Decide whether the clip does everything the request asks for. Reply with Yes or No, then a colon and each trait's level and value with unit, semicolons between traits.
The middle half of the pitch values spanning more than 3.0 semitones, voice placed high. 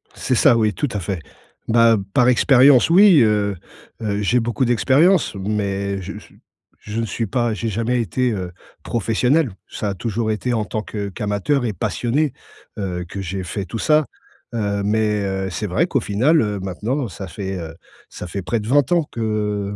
No: average, 3.6 semitones; low, 110 Hz